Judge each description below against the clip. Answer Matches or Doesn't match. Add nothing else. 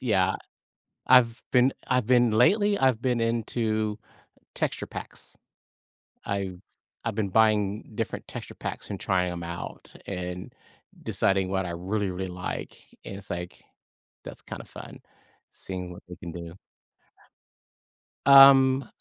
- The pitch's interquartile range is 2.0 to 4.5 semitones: Doesn't match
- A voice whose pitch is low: Matches